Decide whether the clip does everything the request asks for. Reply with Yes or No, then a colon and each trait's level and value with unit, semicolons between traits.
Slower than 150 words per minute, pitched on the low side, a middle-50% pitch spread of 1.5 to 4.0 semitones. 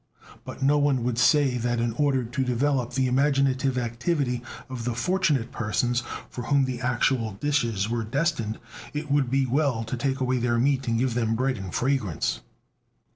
No: average, 180 wpm; low, 125 Hz; average, 2.7 semitones